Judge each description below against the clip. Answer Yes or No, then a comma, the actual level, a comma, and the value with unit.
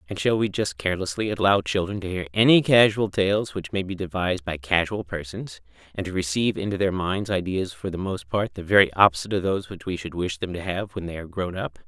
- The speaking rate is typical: No, fast, 235 wpm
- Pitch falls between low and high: No, very low, 95 Hz